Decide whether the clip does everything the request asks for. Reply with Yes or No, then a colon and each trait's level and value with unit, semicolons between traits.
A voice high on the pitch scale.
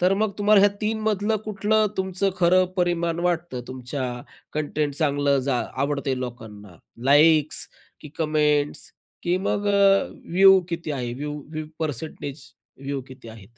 No: medium, 155 Hz